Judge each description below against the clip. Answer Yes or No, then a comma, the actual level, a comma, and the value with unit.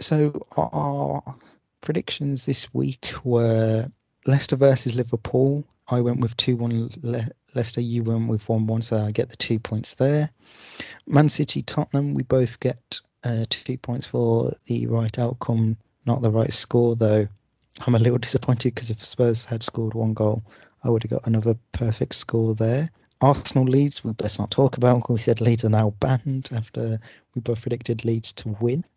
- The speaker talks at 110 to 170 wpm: No, average, 180 wpm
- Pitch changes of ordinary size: No, narrow, 2.3 semitones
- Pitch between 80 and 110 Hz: No, low, 120 Hz